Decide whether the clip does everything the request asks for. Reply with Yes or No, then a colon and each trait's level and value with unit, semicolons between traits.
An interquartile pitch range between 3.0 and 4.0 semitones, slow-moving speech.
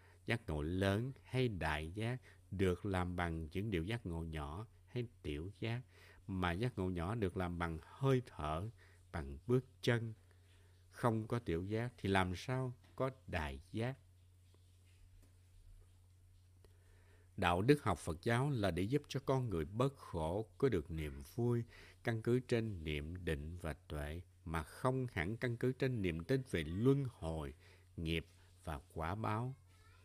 No: average, 5.1 semitones; slow, 155 wpm